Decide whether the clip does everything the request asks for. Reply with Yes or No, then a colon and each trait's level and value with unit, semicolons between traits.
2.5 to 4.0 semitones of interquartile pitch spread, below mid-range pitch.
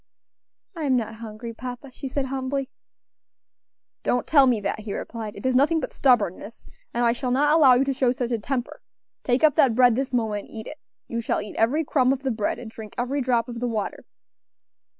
No: average, 2.8 semitones; high, 245 Hz